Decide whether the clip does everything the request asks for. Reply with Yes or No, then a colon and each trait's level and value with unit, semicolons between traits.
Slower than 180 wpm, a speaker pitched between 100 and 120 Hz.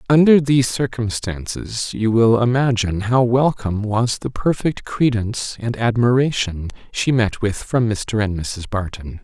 Yes: average, 145 wpm; low, 115 Hz